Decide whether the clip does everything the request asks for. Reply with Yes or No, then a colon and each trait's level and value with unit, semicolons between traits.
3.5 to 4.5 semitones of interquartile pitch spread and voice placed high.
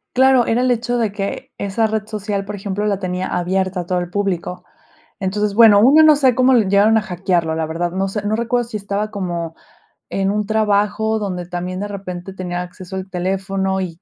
No: average, 2.9 semitones; high, 200 Hz